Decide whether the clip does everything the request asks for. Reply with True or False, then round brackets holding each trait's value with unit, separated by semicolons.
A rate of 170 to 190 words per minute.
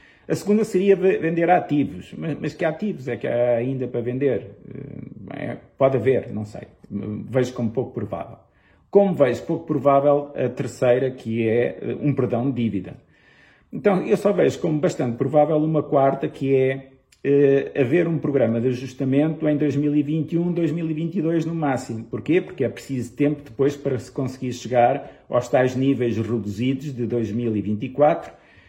False (155 wpm)